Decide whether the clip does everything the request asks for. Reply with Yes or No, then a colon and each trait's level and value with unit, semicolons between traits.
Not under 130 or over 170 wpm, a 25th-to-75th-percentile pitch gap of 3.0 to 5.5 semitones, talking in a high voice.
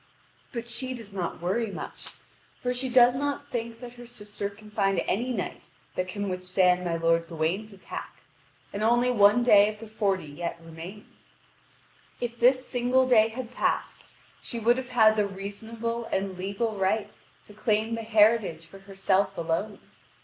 Yes: average, 165 wpm; average, 3.7 semitones; high, 215 Hz